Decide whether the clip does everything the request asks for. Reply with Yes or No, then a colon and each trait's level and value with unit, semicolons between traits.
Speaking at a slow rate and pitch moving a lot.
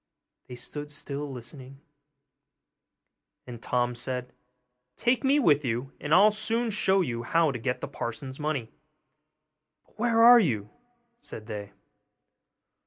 Yes: slow, 130 wpm; wide, 8.2 semitones